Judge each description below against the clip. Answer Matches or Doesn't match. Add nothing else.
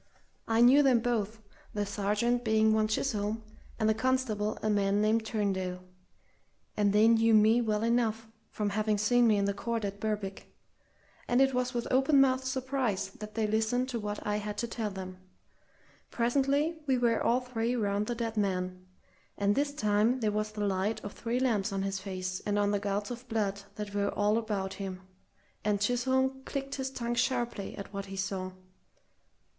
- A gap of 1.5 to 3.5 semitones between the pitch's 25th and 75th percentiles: Matches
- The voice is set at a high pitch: Matches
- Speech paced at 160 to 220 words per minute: Matches